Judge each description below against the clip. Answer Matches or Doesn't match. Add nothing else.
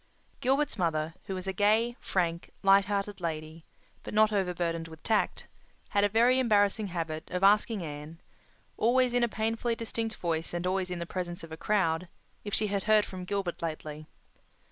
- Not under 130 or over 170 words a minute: Doesn't match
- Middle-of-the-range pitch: Doesn't match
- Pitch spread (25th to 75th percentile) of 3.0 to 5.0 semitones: Matches